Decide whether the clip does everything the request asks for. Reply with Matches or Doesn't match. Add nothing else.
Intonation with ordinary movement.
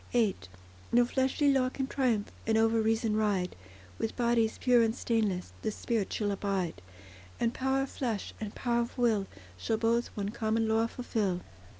Doesn't match